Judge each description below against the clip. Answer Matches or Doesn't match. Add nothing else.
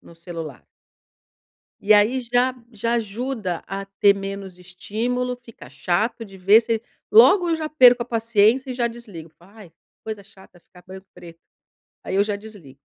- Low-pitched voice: Doesn't match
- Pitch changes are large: Doesn't match